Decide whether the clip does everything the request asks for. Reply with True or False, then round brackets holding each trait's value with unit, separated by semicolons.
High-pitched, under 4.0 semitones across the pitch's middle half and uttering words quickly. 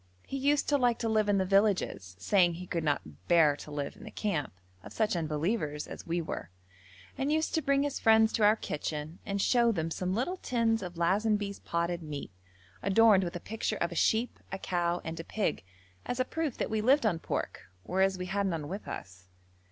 False (195 Hz; 5.2 semitones; 215 wpm)